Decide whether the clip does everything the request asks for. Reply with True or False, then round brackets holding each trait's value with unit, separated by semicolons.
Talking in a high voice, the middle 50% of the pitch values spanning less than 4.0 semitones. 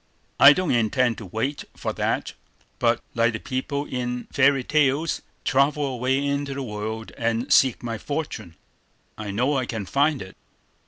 False (130 Hz; 3.6 semitones)